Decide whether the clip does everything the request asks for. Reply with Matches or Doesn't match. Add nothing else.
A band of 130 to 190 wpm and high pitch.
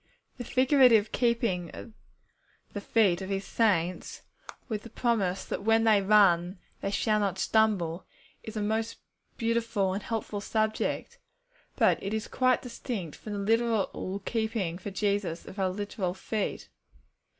Matches